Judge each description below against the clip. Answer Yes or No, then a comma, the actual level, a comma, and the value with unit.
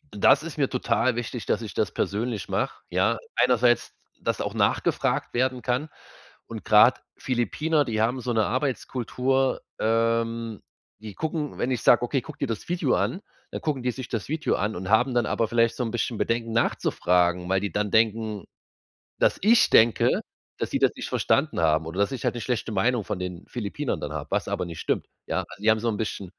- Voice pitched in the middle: No, low, 115 Hz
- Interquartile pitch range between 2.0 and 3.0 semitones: No, average, 3.4 semitones